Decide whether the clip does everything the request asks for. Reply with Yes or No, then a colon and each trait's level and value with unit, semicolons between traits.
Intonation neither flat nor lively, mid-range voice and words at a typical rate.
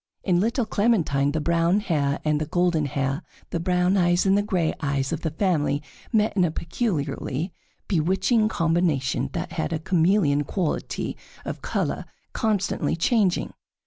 Yes: average, 4.4 semitones; medium, 170 Hz; average, 150 wpm